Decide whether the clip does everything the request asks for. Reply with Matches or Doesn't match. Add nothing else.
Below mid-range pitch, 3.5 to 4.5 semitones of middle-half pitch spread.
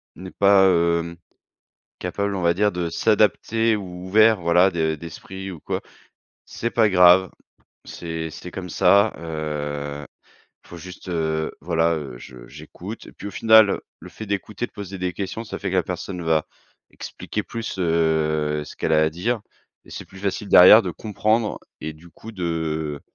Matches